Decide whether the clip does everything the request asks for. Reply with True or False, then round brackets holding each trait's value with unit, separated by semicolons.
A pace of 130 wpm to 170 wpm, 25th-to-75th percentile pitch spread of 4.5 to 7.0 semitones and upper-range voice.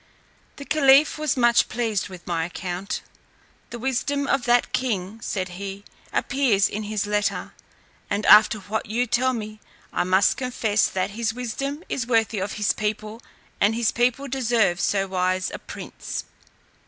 False (155 wpm; 3.7 semitones; 220 Hz)